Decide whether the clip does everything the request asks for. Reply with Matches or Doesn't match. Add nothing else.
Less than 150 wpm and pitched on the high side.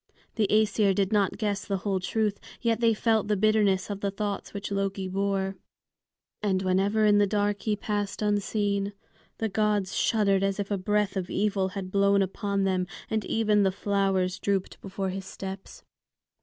Doesn't match